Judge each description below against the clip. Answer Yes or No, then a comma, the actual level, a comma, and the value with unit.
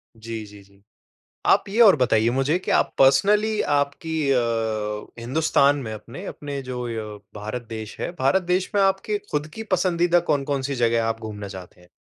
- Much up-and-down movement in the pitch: Yes, wide, 7.3 semitones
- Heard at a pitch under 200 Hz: Yes, low, 135 Hz